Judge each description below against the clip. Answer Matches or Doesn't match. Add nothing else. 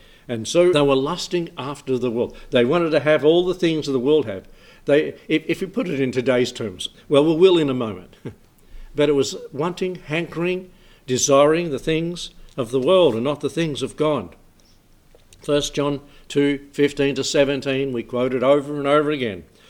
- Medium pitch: Matches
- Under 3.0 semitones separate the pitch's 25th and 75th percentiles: Doesn't match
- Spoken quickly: Doesn't match